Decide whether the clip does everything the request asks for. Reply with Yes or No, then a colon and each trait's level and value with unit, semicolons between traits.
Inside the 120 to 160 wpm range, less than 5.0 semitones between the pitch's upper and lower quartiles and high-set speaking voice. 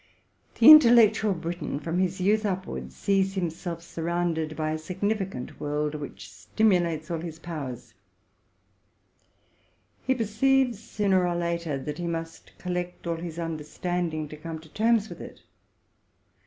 No: average, 140 wpm; average, 3.7 semitones; medium, 175 Hz